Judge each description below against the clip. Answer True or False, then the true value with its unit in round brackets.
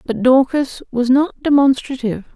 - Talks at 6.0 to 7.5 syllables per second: False (5.1 syllables/s)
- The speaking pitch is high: True (265 Hz)